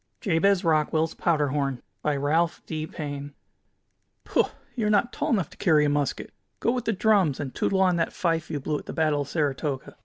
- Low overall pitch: No, medium, 155 Hz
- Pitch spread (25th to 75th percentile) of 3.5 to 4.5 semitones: Yes, average, 4.0 semitones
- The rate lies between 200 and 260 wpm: Yes, fast, 205 wpm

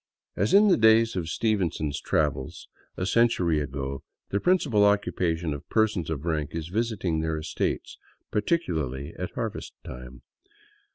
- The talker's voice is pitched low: Yes, very low, 85 Hz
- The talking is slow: No, average, 145 wpm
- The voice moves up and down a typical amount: No, wide, 6.4 semitones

